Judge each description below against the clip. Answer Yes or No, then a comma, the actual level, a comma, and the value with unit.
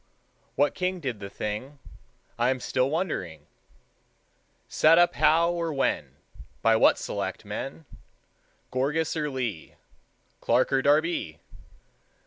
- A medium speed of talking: No, slow, 115 wpm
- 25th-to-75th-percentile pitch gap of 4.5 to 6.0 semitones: Yes, average, 5.1 semitones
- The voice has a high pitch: No, medium, 140 Hz